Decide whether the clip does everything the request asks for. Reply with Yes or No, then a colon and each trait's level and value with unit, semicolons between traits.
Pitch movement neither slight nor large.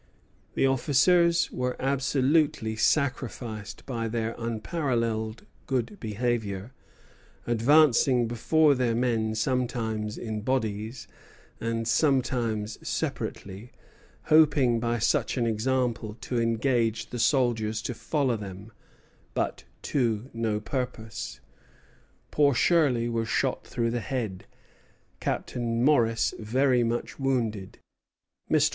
Yes: average, 3.0 semitones